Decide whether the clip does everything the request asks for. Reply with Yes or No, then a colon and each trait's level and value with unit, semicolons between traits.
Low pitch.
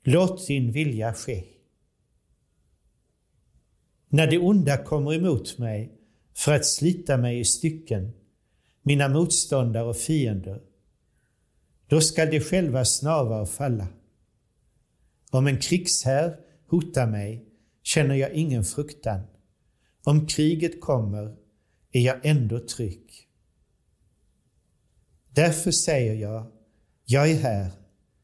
Yes: low, 130 Hz